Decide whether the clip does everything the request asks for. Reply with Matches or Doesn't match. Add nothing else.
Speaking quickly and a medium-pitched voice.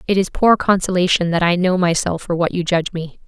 Matches